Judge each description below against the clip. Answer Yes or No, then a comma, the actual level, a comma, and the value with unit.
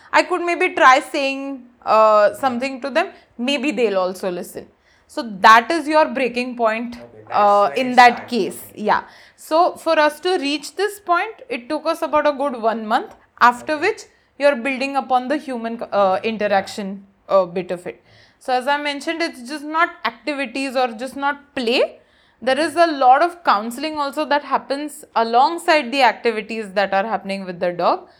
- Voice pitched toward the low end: No, very high, 270 Hz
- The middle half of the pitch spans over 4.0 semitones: Yes, wide, 5.4 semitones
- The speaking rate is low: No, average, 175 wpm